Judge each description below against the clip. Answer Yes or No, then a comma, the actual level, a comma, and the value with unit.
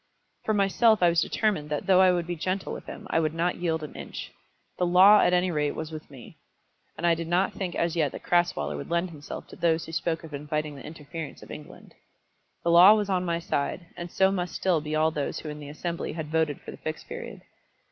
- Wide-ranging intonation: No, average, 2.7 semitones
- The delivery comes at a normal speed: No, fast, 240 wpm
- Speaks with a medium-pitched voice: Yes, medium, 170 Hz